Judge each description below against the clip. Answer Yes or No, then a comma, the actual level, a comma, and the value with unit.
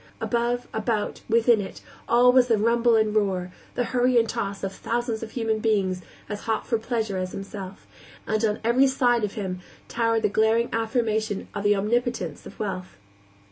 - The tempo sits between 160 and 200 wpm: Yes, average, 180 wpm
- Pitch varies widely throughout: No, narrow, 2.5 semitones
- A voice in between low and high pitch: No, high, 220 Hz